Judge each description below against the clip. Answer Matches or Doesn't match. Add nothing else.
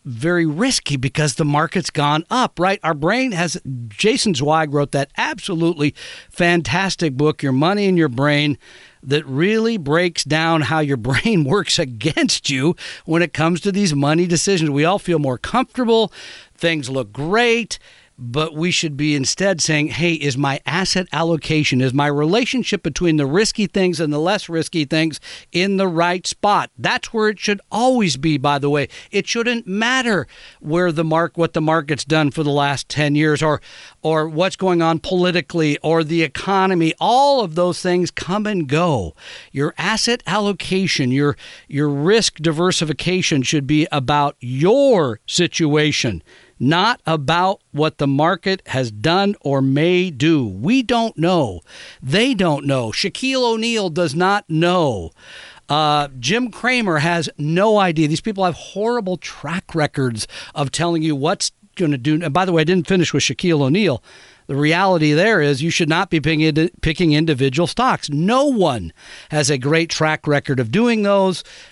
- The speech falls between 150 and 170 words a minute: Matches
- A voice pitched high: Doesn't match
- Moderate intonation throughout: Matches